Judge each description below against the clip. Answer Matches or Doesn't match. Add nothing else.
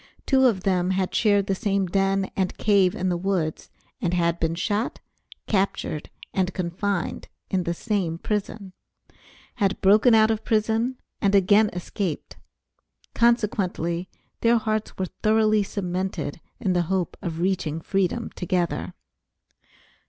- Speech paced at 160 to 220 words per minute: Doesn't match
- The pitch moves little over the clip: Doesn't match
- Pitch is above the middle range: Matches